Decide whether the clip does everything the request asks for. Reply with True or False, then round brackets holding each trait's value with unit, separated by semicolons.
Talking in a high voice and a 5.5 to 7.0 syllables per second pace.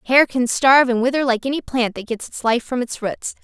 True (245 Hz; 5.6 syllables/s)